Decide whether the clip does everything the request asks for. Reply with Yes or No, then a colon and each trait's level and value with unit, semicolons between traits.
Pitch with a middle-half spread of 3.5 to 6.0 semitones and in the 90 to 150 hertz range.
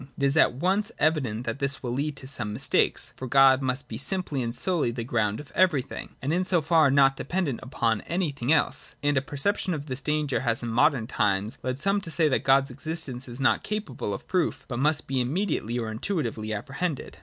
Yes: average, 4.5 semitones; low, 135 Hz